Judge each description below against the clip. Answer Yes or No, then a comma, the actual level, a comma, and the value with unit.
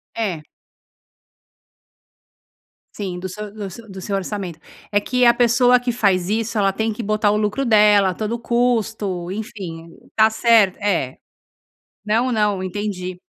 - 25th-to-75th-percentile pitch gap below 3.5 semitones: Yes, average, 3.0 semitones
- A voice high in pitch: Yes, high, 210 Hz